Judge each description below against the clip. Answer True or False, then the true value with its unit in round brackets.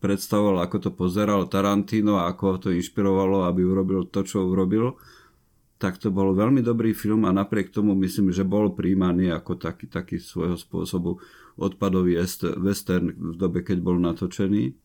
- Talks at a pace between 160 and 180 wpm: True (165 wpm)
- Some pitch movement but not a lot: False (2.1 semitones)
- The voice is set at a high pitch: False (95 Hz)